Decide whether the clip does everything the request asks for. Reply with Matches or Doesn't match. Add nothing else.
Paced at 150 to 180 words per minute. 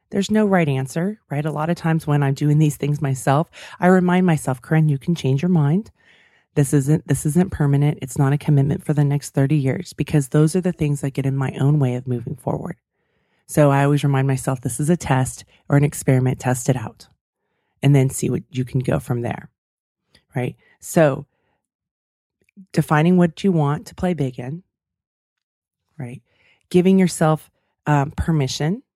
Doesn't match